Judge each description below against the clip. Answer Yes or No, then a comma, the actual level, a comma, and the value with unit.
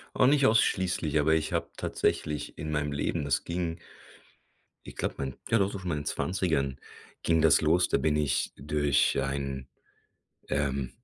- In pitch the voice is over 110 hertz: No, very low, 75 Hz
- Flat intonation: No, average, 3.7 semitones